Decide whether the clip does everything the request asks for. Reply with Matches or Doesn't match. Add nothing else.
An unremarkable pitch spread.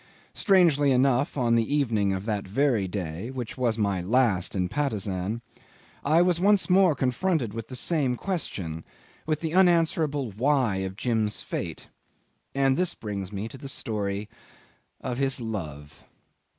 Doesn't match